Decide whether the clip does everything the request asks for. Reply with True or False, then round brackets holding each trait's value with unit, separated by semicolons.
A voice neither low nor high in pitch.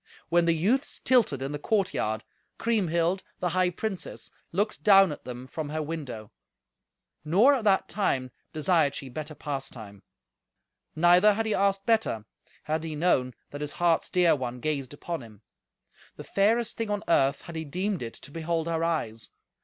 True (165 Hz)